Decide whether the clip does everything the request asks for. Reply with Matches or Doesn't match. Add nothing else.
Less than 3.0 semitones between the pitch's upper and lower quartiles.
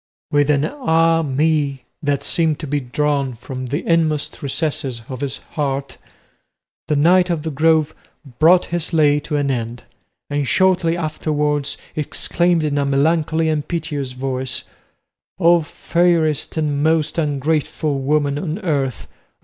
Matches